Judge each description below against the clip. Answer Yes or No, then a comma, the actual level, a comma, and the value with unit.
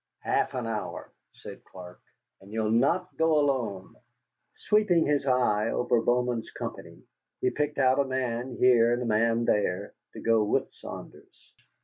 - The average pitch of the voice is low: Yes, low, 120 Hz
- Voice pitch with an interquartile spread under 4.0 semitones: Yes, average, 3.3 semitones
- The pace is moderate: Yes, average, 150 wpm